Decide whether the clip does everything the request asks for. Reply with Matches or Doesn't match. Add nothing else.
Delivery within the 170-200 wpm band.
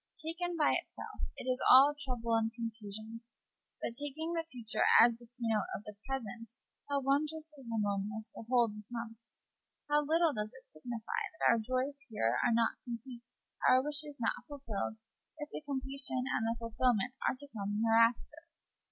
Doesn't match